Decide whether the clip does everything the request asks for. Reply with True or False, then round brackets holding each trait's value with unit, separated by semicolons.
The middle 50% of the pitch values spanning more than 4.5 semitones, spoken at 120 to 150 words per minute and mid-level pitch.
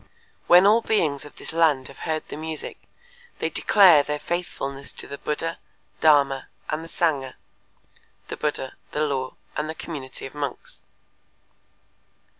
False (2.9 semitones; 145 wpm; 150 Hz)